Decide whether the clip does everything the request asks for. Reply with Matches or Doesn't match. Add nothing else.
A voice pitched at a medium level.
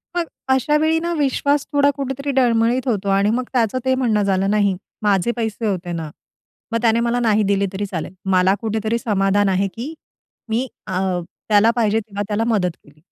Doesn't match